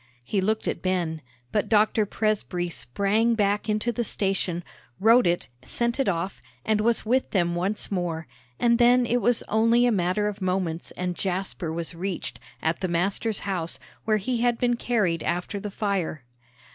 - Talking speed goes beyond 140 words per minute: Yes, average, 170 wpm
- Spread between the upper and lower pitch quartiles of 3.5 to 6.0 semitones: Yes, average, 4.1 semitones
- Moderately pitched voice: No, high, 200 Hz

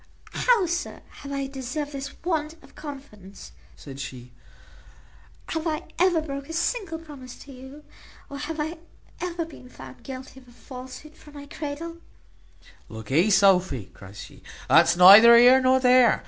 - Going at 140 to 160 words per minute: Yes, average, 155 wpm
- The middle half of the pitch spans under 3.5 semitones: No, average, 5.1 semitones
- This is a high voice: Yes, very high, 275 Hz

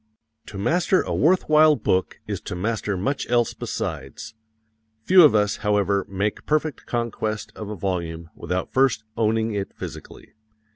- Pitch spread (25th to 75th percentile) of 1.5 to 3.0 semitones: No, average, 5.0 semitones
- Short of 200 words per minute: Yes, average, 150 wpm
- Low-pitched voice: Yes, low, 110 Hz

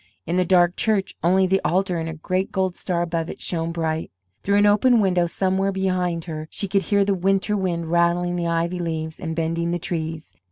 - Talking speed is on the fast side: Yes, fast, 210 wpm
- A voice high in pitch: No, medium, 175 Hz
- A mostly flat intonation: Yes, narrow, 2.3 semitones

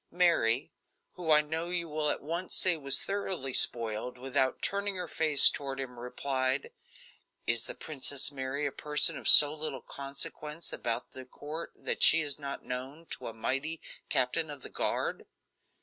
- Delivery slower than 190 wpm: Yes, average, 165 wpm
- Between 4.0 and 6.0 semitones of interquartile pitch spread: No, average, 3.5 semitones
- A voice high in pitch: No, medium, 145 Hz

